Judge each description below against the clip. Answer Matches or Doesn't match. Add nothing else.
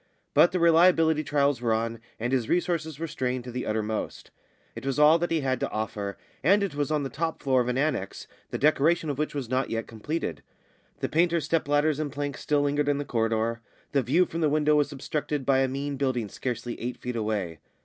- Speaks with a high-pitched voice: Doesn't match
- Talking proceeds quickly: Matches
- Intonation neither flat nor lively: Matches